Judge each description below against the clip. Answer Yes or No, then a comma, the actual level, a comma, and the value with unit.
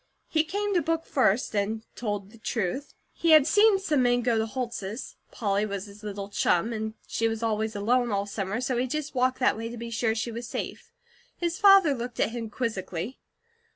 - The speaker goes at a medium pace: No, fast, 210 wpm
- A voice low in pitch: No, high, 230 Hz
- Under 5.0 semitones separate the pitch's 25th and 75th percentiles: Yes, average, 3.6 semitones